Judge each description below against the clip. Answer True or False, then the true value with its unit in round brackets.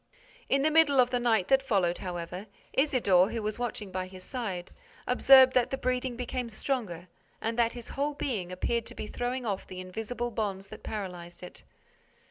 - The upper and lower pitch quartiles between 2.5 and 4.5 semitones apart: False (5.2 semitones)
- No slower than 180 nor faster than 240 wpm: True (185 wpm)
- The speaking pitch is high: True (225 Hz)